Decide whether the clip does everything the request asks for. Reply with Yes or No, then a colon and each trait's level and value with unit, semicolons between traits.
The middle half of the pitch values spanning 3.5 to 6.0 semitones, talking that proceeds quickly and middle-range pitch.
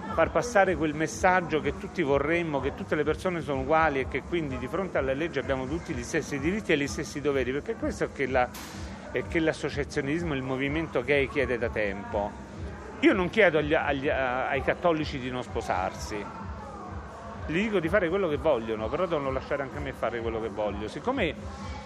Yes: average, 4.0 semitones; fast, 195 wpm; medium, 145 Hz